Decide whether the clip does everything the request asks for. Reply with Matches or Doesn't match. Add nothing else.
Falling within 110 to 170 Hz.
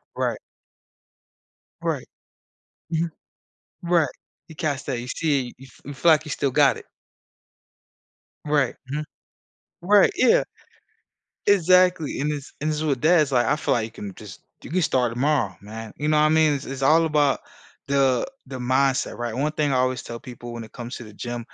Matches